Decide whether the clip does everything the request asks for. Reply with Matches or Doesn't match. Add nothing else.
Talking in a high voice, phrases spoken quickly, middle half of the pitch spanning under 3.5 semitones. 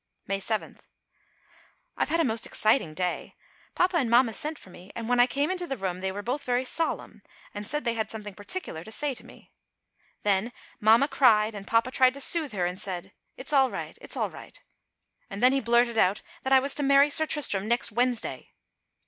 Doesn't match